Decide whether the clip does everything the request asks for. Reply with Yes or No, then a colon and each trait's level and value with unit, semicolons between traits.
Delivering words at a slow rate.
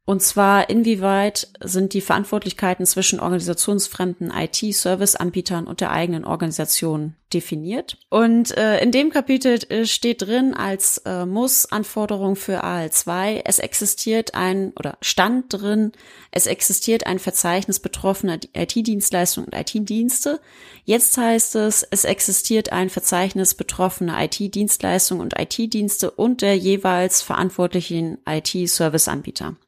Yes: slow, 115 wpm